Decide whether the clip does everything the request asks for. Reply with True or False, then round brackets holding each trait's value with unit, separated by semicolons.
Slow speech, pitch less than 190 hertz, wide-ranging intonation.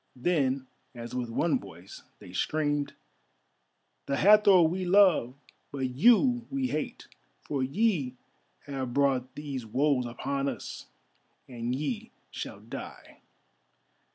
True (115 wpm; 140 Hz; 5.8 semitones)